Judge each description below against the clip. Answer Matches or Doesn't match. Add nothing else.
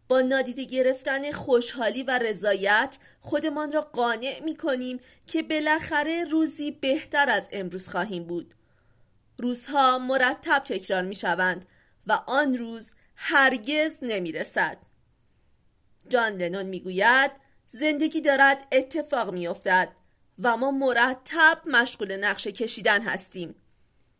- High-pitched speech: Matches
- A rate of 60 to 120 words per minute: Matches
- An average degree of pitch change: Doesn't match